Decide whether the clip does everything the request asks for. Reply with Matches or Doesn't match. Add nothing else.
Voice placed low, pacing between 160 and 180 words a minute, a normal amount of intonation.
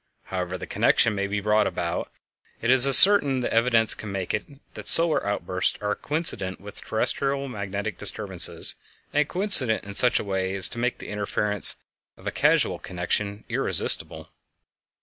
Matches